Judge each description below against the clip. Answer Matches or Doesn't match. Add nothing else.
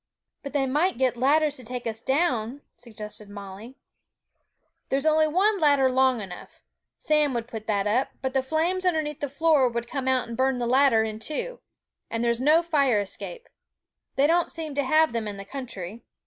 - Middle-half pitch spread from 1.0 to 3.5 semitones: Doesn't match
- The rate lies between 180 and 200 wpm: Matches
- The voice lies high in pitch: Matches